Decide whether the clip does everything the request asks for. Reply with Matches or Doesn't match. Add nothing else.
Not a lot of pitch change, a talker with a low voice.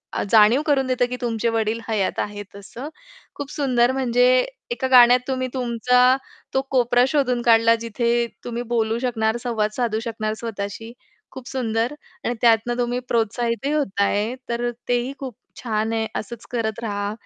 Doesn't match